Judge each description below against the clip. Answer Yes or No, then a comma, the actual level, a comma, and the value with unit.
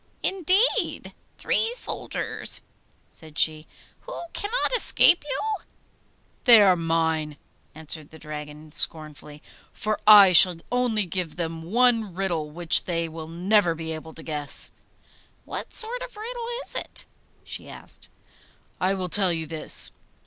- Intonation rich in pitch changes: Yes, wide, 7.0 semitones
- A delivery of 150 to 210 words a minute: No, slow, 135 wpm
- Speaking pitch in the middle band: Yes, medium, 175 Hz